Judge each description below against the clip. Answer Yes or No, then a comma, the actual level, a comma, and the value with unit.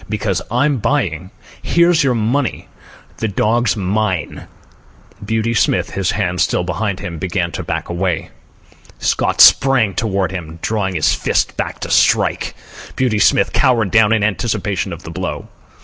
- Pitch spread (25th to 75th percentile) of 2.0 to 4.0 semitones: Yes, average, 3.6 semitones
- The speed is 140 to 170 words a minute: Yes, average, 150 wpm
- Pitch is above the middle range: No, low, 105 Hz